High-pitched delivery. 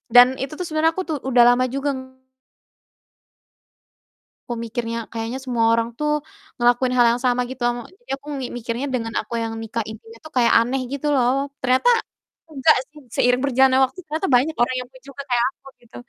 Yes: very high, 255 Hz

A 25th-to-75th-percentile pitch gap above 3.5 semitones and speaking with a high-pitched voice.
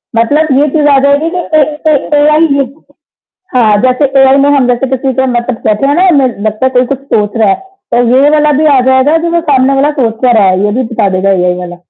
Yes: average, 4.4 semitones; very high, 265 Hz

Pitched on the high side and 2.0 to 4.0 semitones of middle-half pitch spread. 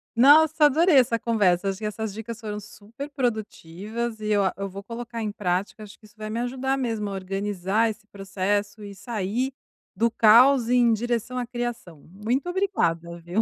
Yes: high, 220 Hz; average, 3.2 semitones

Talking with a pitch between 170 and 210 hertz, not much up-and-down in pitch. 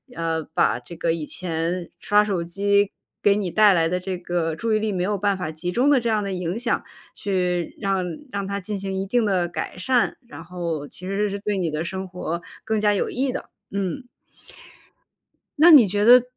No: high, 190 Hz; average, 3.1 semitones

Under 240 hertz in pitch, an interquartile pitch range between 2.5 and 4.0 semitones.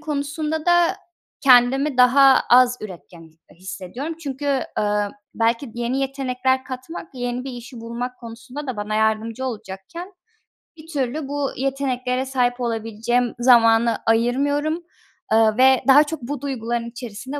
No: very high, 250 Hz; average, 3.3 semitones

